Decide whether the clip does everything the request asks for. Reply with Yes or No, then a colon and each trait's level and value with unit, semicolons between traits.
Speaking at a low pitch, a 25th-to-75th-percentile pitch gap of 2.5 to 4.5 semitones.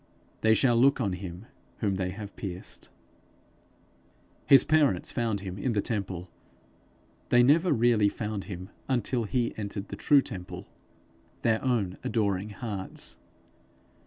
Yes: low, 105 Hz; average, 3.9 semitones